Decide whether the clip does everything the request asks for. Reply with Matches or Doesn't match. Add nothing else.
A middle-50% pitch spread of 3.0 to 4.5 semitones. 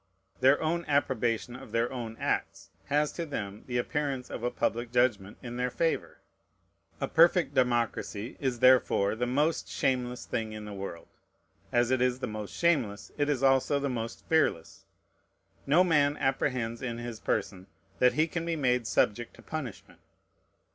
Matches